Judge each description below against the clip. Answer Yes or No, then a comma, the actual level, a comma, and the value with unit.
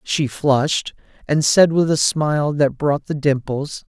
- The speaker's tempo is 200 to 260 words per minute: No, average, 165 wpm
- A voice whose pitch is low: No, medium, 145 Hz